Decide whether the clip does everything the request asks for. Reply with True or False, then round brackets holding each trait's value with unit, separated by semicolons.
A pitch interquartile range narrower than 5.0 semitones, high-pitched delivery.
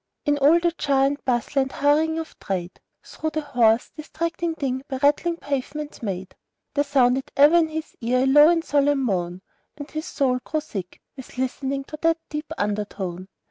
True (3.8 semitones; 280 Hz)